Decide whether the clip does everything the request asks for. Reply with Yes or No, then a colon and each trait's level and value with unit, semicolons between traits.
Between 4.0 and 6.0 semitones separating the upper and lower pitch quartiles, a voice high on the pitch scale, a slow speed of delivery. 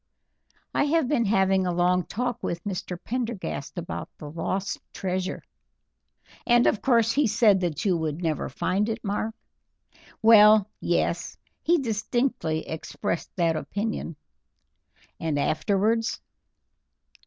Yes: average, 4.7 semitones; high, 200 Hz; slow, 120 wpm